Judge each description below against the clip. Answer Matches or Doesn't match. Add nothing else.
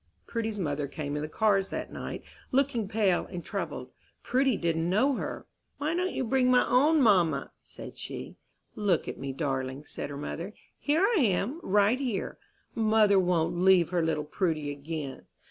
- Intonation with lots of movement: Matches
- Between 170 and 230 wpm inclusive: Matches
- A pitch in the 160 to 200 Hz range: Matches